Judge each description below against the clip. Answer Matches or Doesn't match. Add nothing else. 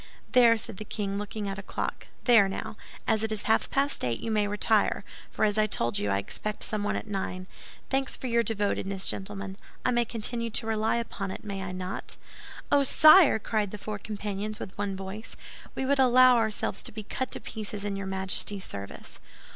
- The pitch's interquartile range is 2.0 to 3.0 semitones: Matches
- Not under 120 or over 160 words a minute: Doesn't match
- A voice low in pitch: Doesn't match